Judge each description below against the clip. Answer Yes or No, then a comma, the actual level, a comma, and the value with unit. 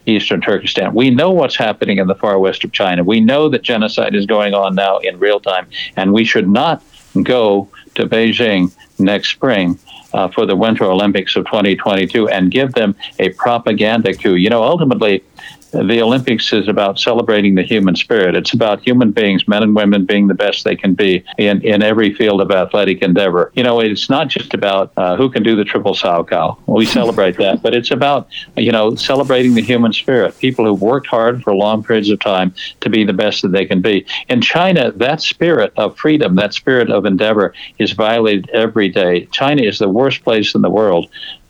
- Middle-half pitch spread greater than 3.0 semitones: No, narrow, 2.6 semitones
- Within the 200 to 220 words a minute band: Yes, fast, 205 wpm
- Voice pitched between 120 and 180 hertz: No, low, 105 Hz